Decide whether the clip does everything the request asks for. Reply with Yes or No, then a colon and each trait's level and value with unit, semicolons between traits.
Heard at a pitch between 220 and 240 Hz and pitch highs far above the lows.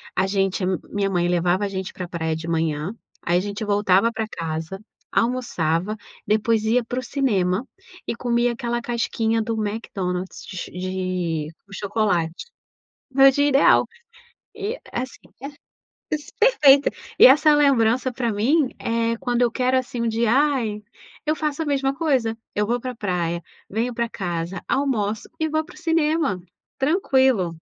Yes: high, 225 Hz; wide, 5.8 semitones